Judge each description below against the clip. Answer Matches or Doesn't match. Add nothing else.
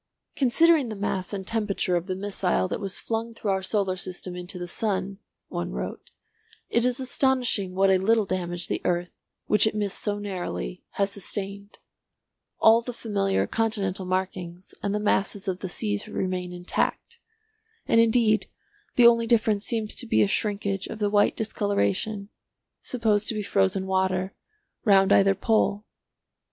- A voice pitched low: Doesn't match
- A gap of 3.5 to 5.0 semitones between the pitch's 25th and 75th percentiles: Doesn't match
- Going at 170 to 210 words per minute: Doesn't match